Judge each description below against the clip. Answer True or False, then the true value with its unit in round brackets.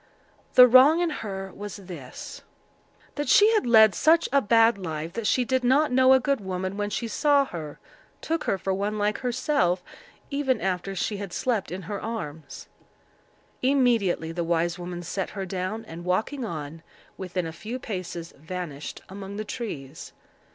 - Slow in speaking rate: False (165 wpm)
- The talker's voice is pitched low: False (200 Hz)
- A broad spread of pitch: True (6.0 semitones)